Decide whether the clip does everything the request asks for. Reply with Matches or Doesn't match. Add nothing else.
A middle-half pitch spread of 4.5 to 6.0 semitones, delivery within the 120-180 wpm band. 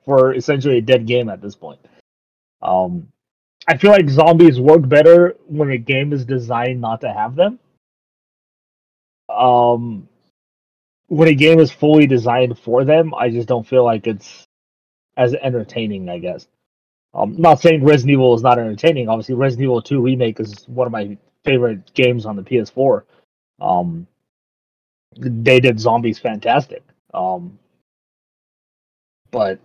Matches